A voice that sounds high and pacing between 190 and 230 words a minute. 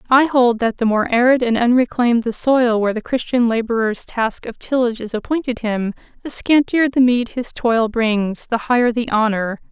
No: high, 235 Hz; average, 180 wpm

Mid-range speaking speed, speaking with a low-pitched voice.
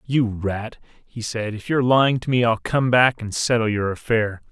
No: fast, 215 wpm; low, 115 Hz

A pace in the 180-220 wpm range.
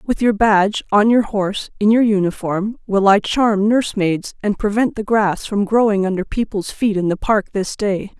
Yes: fast, 205 wpm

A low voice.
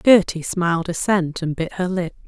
No: medium, 175 Hz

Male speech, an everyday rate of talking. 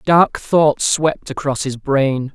Yes: male; average, 155 wpm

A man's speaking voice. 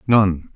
Yes: male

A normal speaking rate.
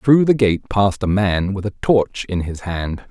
No: fast, 230 wpm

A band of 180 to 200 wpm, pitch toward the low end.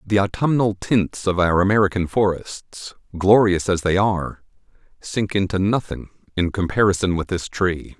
No: average, 145 wpm; very low, 95 Hz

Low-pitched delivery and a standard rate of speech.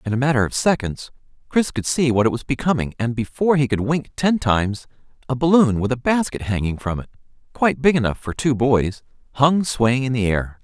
No: low, 130 Hz; fast, 215 wpm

